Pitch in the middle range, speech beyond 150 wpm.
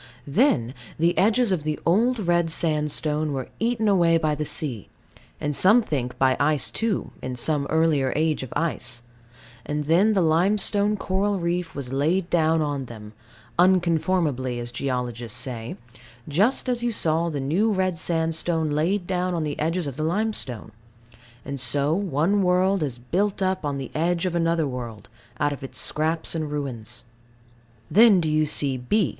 Yes: medium, 160 Hz; average, 165 wpm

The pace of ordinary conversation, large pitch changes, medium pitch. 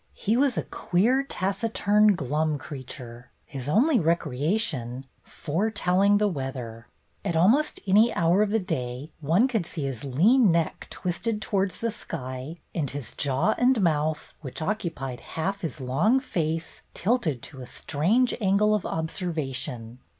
Yes: average, 150 wpm; wide, 7.4 semitones; medium, 170 Hz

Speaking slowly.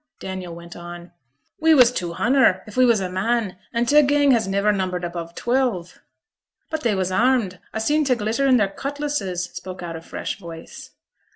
No: average, 190 wpm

